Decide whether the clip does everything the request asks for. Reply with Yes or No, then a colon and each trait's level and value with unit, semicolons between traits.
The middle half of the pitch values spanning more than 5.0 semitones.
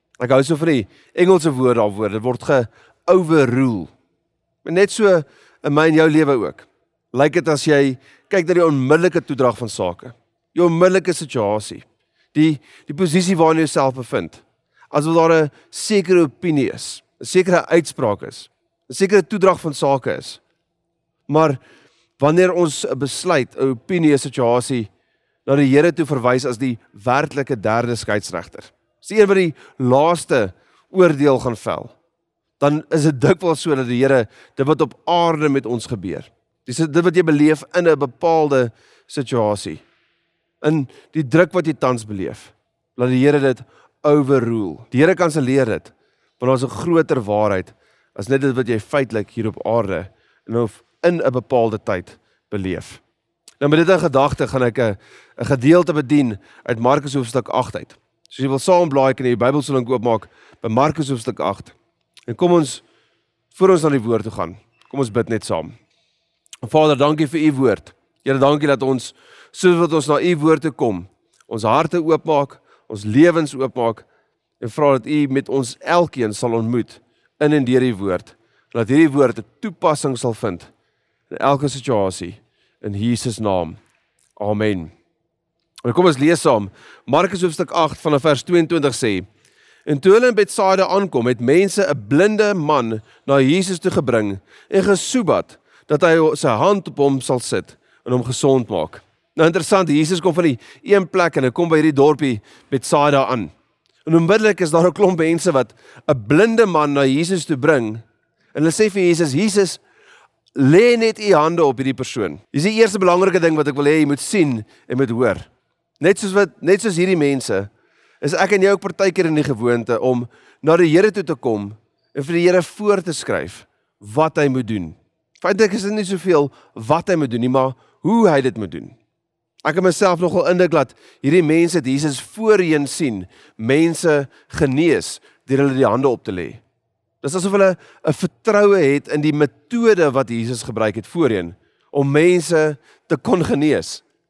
Yes: wide, 5.5 semitones